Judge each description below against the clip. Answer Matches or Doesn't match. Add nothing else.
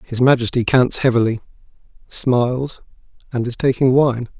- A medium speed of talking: Doesn't match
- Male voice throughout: Matches